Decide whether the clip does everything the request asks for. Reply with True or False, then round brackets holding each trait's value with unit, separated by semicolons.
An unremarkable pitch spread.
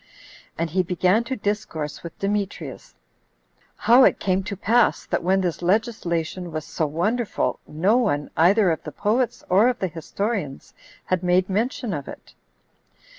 True (4.3 semitones)